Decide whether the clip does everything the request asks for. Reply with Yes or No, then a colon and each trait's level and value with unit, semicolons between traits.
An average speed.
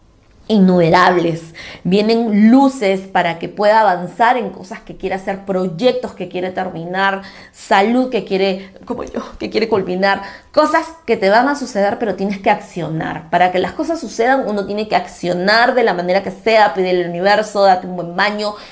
No: fast, 175 wpm